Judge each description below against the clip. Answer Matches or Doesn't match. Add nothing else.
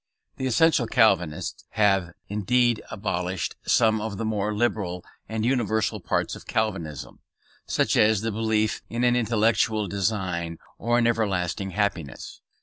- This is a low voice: Matches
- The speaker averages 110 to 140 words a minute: Matches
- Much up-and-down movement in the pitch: Doesn't match